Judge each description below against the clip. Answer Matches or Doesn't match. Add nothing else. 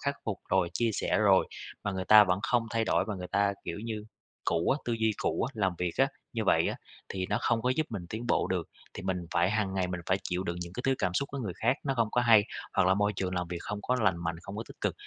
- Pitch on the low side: Matches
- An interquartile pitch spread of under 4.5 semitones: Matches